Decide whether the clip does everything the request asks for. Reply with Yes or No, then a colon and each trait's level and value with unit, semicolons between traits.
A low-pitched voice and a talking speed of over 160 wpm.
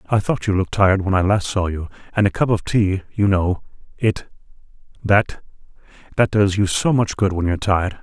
Yes: low, 100 Hz; average, 195 wpm